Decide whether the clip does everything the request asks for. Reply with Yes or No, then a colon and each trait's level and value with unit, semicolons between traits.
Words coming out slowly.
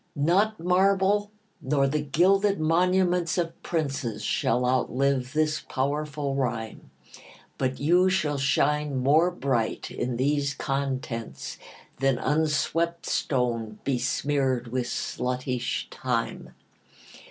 Yes: slow, 100 wpm